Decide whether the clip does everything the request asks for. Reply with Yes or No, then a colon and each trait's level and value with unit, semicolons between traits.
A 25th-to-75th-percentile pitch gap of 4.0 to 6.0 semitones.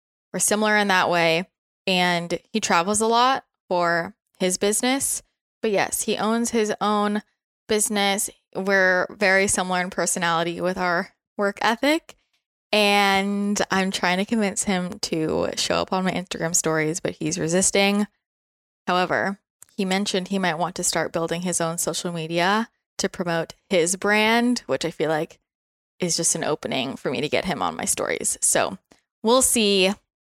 No: average, 3.3 semitones